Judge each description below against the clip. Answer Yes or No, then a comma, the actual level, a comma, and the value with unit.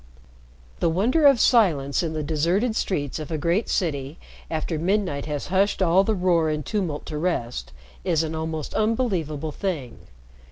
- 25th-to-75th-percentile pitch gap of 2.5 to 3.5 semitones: No, average, 4.2 semitones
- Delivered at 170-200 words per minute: No, average, 160 wpm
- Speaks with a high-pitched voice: No, medium, 165 Hz